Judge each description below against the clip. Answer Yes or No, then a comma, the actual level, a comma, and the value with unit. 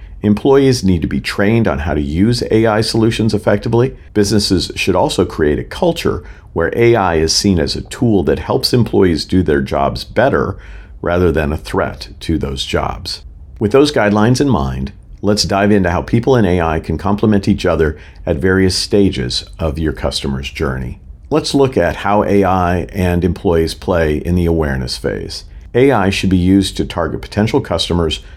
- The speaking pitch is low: Yes, very low, 95 Hz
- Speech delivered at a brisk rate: No, average, 175 wpm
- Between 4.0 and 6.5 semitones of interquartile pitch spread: Yes, average, 4.4 semitones